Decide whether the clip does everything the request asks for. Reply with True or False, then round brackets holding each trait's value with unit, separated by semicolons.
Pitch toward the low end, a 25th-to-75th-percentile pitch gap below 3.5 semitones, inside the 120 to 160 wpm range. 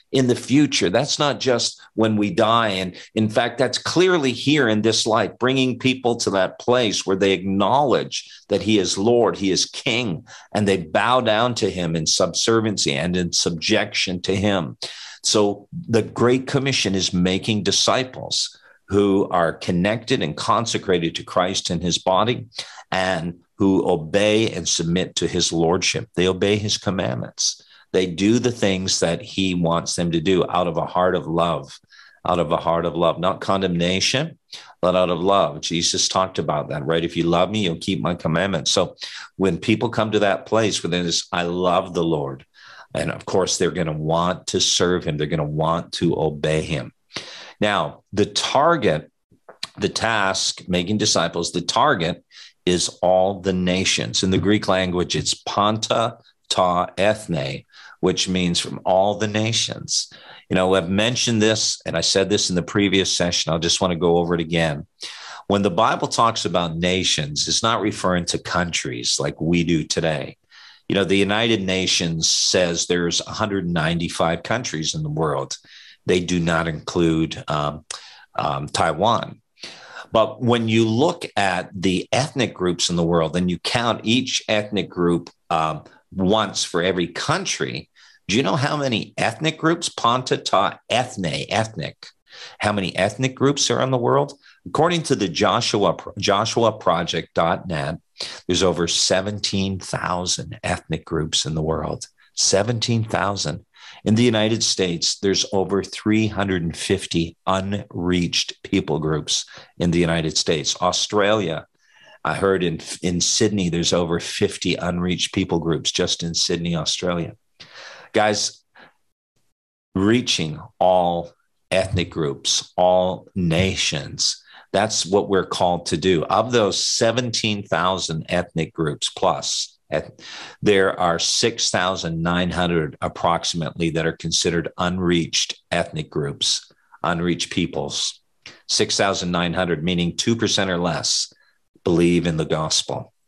False (95 Hz; 3.9 semitones; 150 wpm)